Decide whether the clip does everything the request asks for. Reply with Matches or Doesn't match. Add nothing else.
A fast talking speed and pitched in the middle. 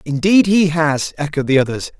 Doesn't match